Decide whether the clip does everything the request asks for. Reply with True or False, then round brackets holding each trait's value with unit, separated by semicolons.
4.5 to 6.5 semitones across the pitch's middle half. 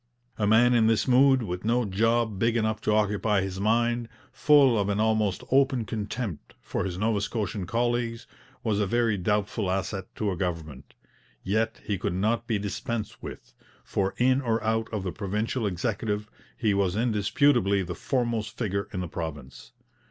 False (3.0 semitones)